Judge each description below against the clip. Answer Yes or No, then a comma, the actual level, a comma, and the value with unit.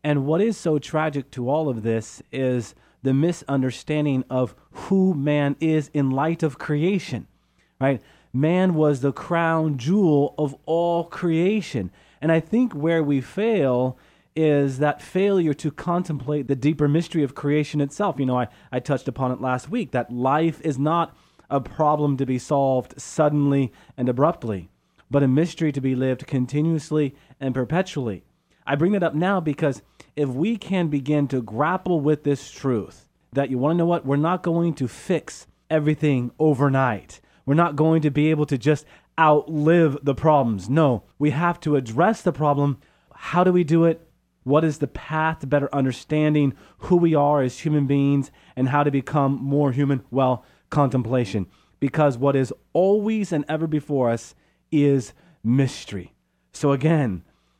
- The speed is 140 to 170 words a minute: Yes, average, 165 wpm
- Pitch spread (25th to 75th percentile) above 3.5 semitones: No, average, 3.2 semitones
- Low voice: No, medium, 145 Hz